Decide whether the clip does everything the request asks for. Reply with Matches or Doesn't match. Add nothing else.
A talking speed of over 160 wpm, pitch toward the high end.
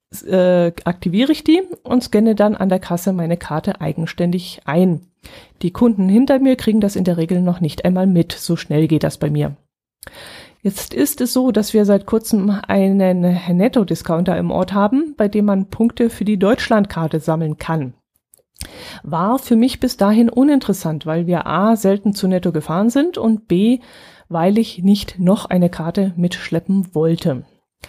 Matches